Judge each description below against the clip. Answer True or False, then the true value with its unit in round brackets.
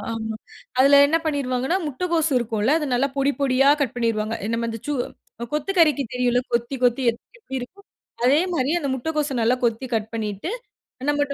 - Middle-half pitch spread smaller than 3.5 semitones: False (4.0 semitones)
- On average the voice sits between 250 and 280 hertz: True (265 Hz)